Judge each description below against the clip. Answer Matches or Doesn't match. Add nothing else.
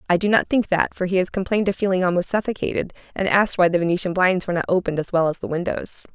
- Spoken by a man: Doesn't match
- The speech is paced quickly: Matches